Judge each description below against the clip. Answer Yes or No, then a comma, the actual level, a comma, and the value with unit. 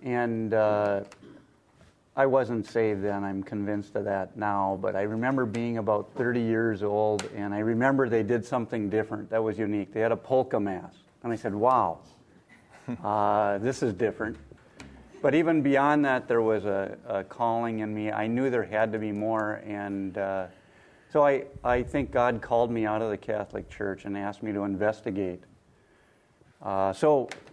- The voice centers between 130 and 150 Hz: No, low, 110 Hz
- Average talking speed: Yes, average, 175 wpm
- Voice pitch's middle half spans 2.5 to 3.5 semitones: Yes, average, 2.8 semitones